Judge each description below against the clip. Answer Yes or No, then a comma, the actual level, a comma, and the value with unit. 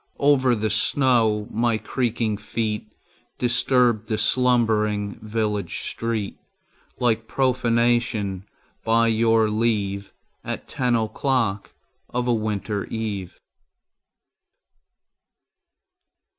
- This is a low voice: Yes, low, 110 Hz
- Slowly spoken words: Yes, slow, 85 wpm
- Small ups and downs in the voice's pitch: Yes, narrow, 2.3 semitones